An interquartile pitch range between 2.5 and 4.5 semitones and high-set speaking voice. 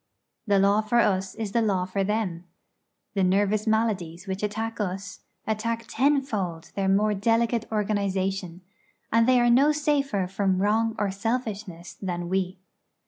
Yes: average, 2.9 semitones; high, 205 Hz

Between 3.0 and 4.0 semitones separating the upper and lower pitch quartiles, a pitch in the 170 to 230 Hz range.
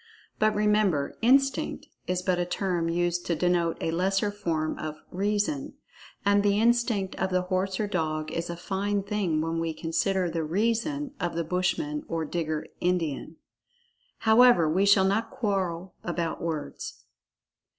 Yes: average, 3.7 semitones; medium, 185 Hz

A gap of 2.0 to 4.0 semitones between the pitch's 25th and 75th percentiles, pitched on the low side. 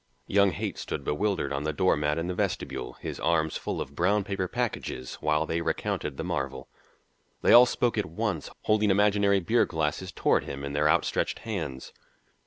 No: wide, 5.5 semitones; very low, 85 Hz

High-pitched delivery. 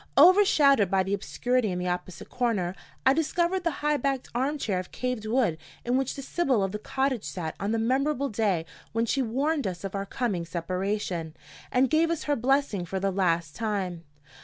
Yes: high, 225 Hz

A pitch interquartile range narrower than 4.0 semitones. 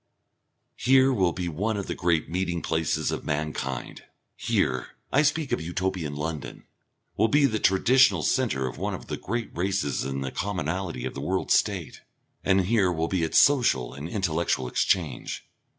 No: average, 5.0 semitones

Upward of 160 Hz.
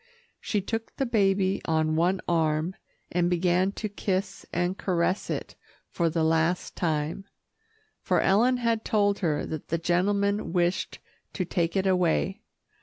Yes: medium, 185 Hz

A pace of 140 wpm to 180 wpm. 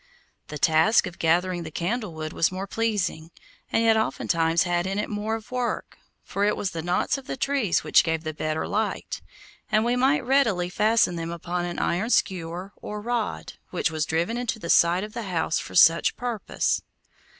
No: average, 195 wpm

